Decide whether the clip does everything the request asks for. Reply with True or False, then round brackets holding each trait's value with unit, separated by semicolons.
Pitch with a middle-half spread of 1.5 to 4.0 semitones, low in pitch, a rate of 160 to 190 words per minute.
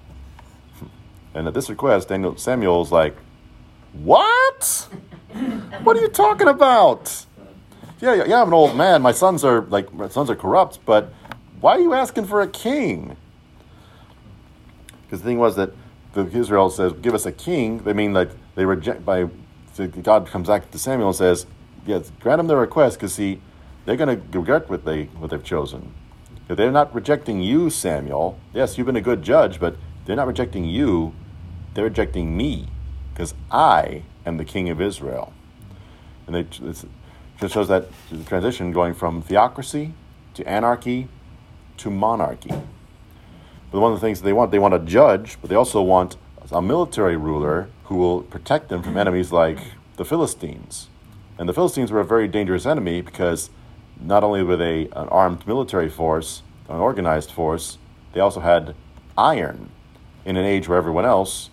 False (5.2 semitones; 95 Hz; 170 wpm)